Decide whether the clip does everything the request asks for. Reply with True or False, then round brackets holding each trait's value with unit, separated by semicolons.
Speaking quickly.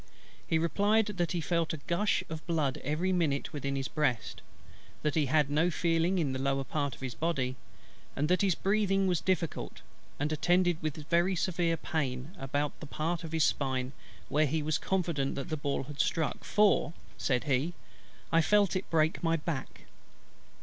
False (180 wpm)